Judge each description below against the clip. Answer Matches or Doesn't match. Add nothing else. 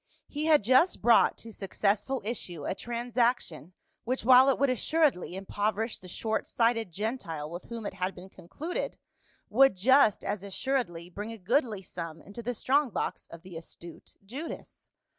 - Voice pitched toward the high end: Matches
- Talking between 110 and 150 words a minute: Doesn't match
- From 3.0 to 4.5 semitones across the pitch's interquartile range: Doesn't match